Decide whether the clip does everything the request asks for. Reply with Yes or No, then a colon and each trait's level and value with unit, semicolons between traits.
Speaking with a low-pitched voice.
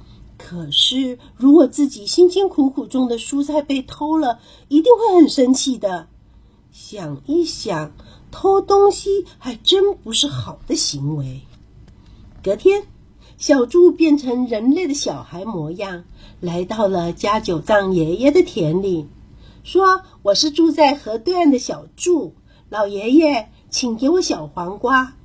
No: very high, 255 Hz